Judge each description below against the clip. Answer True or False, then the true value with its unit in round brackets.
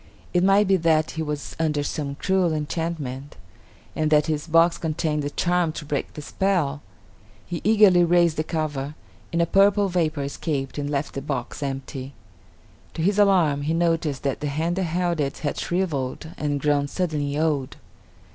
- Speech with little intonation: False (3.2 semitones)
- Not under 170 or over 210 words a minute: True (175 wpm)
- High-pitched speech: False (155 Hz)